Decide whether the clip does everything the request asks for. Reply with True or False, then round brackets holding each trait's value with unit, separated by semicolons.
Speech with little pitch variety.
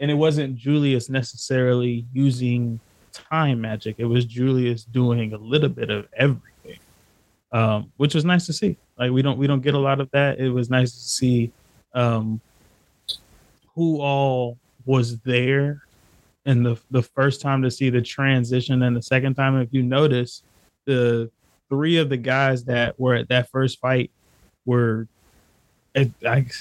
True (2.3 semitones)